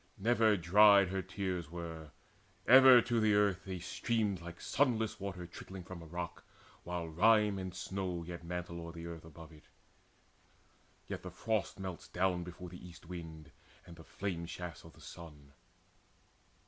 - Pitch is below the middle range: Yes, very low, 90 Hz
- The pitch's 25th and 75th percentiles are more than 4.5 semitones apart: No, average, 2.9 semitones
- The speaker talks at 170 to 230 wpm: No, average, 160 wpm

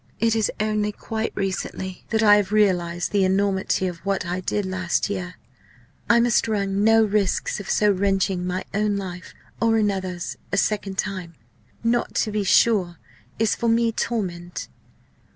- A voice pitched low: No, high, 200 Hz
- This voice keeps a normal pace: Yes, average, 160 wpm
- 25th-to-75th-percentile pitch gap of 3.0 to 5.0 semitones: No, narrow, 2.4 semitones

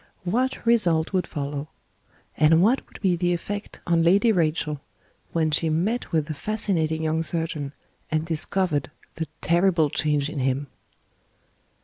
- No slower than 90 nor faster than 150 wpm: Yes, average, 140 wpm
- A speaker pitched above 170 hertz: No, medium, 165 Hz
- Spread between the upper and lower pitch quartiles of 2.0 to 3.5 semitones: Yes, average, 3.1 semitones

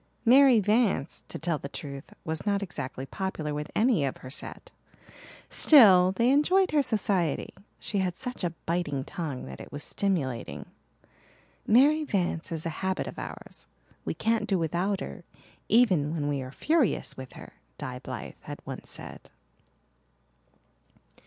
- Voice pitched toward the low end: No, medium, 185 Hz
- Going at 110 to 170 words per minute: Yes, average, 150 wpm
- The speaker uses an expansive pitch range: Yes, wide, 7.1 semitones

